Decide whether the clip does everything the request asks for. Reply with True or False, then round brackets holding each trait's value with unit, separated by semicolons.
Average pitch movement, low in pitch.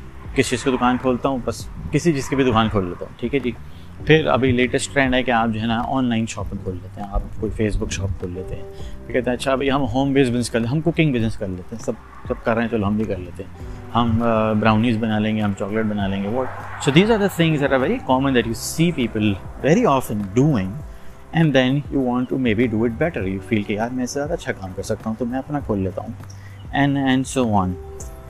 True (4.6 semitones; 115 Hz)